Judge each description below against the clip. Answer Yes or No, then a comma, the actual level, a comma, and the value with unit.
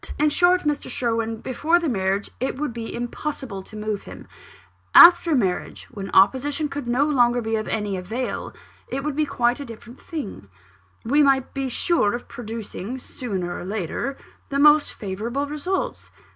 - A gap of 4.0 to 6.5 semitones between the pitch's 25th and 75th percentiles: Yes, average, 5.1 semitones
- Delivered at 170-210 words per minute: No, average, 160 wpm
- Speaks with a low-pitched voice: No, high, 245 Hz